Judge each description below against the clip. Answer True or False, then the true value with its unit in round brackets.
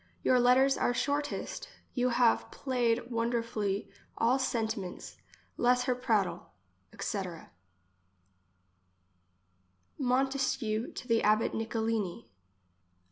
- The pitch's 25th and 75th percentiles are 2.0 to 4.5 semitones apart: True (2.4 semitones)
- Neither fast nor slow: False (90 wpm)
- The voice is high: True (235 Hz)